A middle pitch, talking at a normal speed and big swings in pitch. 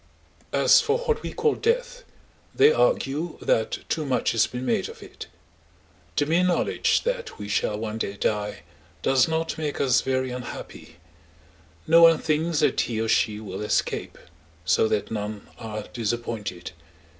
No: low, 130 Hz; average, 155 wpm; wide, 7.9 semitones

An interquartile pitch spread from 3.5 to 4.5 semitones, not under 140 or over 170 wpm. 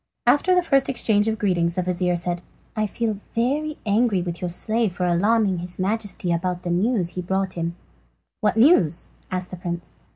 No: average, 4.2 semitones; average, 190 wpm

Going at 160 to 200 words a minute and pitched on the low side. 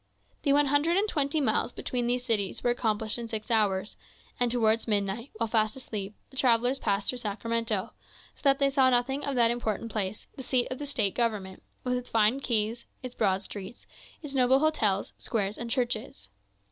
No: average, 190 wpm; high, 235 Hz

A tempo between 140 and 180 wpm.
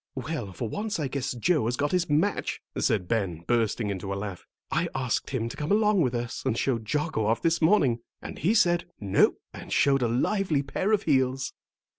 No: fast, 205 wpm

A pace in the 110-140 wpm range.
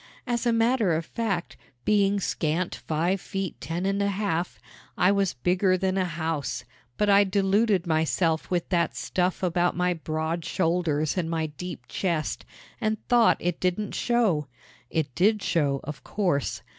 No: average, 155 wpm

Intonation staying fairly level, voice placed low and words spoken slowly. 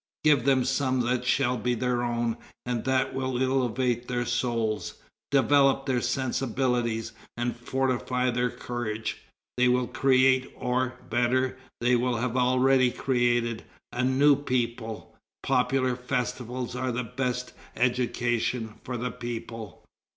Yes: narrow, 1.3 semitones; low, 125 Hz; slow, 125 wpm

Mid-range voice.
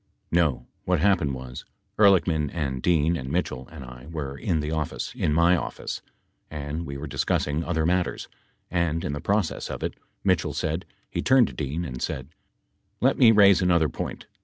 No: very low, 80 Hz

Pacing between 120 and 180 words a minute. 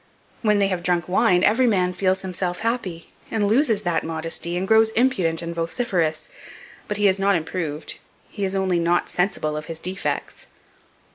Yes: average, 170 wpm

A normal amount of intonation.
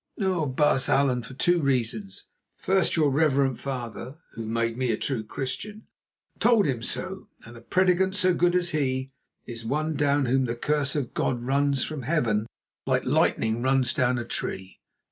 Yes: average, 4.4 semitones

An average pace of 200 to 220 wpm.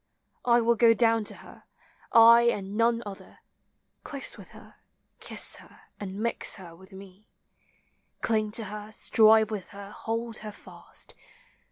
No: average, 150 wpm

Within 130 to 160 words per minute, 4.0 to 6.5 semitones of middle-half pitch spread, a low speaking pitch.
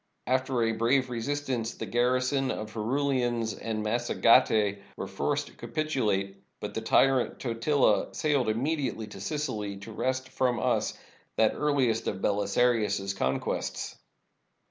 No: slow, 135 wpm; average, 3.4 semitones; low, 120 Hz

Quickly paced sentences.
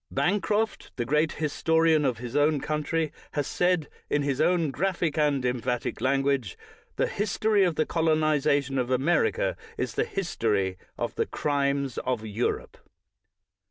No: average, 145 wpm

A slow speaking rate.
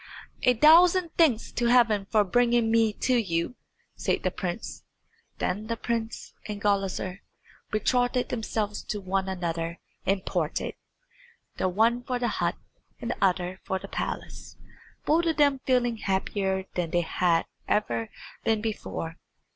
No: average, 145 wpm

